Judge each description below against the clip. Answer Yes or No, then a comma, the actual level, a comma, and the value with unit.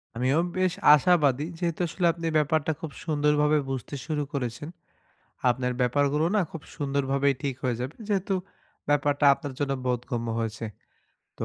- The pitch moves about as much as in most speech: Yes, average, 3.1 semitones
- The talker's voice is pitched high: No, medium, 145 Hz